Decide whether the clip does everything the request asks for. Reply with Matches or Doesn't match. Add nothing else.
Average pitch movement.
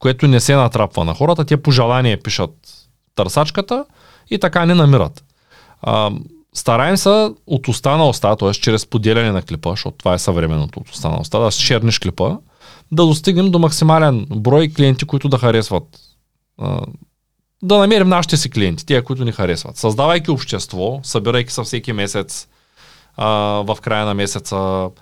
Doesn't match